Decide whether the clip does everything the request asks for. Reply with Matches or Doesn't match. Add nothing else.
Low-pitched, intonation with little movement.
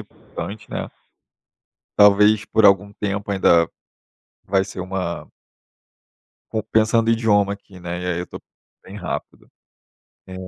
Matches